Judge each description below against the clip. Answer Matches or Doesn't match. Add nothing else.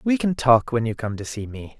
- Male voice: Matches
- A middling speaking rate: Doesn't match